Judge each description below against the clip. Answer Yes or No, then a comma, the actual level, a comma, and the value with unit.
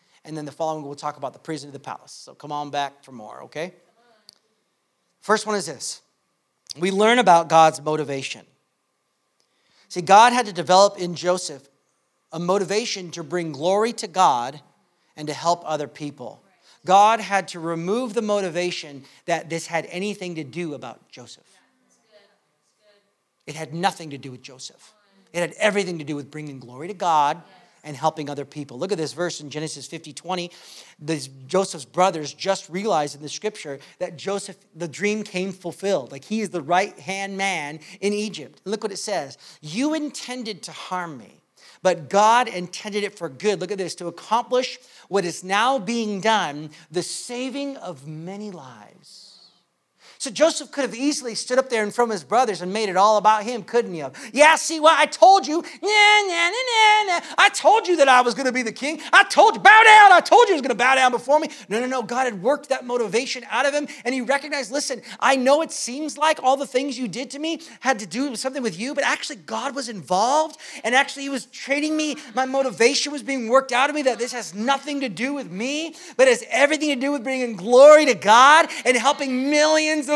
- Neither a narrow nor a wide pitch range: No, wide, 7.9 semitones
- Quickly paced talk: Yes, fast, 210 wpm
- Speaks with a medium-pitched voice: No, high, 210 Hz